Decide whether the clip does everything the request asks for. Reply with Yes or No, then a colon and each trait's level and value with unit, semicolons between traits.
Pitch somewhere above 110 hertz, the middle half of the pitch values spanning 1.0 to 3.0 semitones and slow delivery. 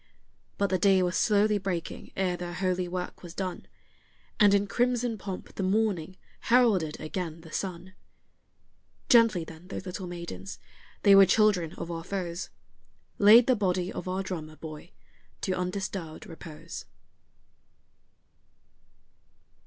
Yes: medium, 185 Hz; average, 2.7 semitones; slow, 130 wpm